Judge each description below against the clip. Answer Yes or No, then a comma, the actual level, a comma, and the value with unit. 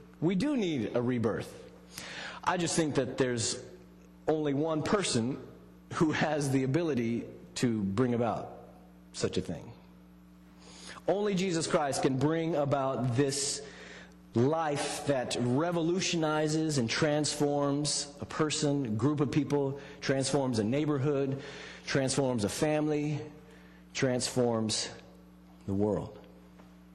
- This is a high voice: No, low, 135 Hz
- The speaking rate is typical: No, slow, 110 wpm